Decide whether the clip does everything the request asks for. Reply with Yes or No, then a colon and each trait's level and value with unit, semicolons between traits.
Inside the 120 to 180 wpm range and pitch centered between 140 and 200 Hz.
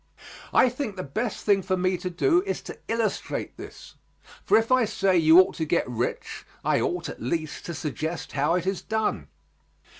No: average, 190 wpm; medium, 185 Hz